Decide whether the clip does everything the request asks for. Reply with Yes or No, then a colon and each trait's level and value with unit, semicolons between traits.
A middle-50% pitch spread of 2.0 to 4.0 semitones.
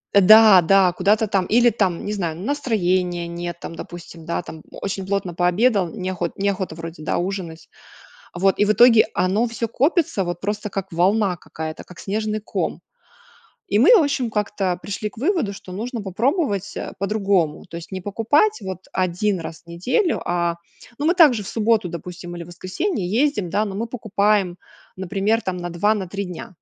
Yes: average, 3.7 semitones